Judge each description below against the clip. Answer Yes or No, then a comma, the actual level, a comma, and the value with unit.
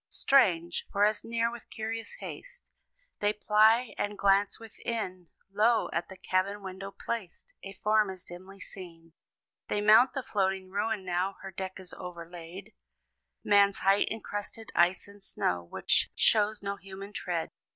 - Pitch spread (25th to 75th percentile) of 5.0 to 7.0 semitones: No, narrow, 2.5 semitones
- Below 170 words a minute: Yes, average, 150 wpm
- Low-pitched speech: No, high, 200 Hz